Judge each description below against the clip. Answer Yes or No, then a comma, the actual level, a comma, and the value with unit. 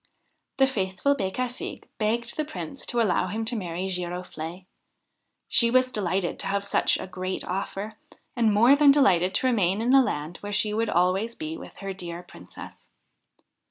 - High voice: Yes, high, 205 Hz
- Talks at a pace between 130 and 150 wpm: No, average, 170 wpm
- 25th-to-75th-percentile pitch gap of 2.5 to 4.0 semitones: No, average, 4.7 semitones